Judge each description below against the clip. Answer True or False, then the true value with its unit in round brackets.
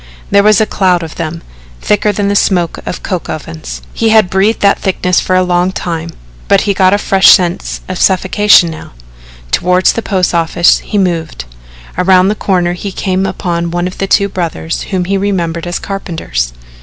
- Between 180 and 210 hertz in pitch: True (185 Hz)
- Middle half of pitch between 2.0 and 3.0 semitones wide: True (2.5 semitones)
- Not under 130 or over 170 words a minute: False (185 wpm)